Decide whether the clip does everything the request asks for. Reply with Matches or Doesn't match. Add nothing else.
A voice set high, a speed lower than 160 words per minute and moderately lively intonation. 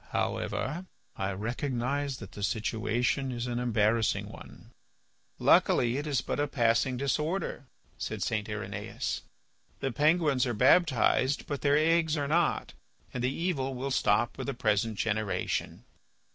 Doesn't match